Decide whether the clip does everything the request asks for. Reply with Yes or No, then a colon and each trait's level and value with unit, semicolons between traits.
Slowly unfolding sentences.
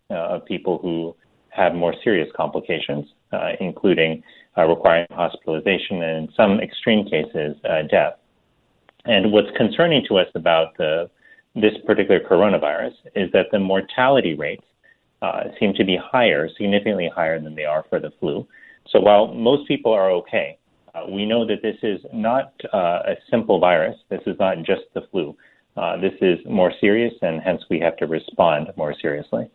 No: average, 170 wpm